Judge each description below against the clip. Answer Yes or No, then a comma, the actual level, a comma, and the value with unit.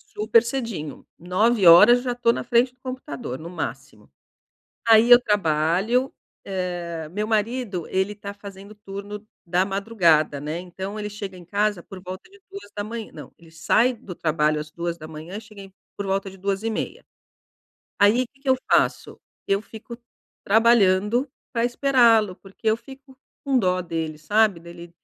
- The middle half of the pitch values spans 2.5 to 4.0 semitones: No, average, 4.8 semitones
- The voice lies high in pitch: Yes, high, 200 Hz